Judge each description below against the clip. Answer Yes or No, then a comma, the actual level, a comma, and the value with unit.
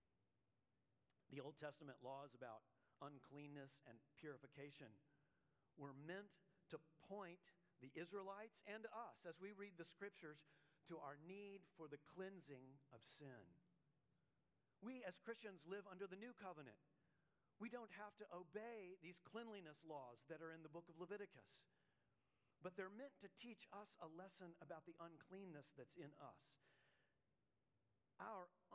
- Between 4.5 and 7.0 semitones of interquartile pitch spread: Yes, wide, 5.6 semitones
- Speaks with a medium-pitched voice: Yes, medium, 165 Hz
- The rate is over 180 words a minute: No, average, 140 wpm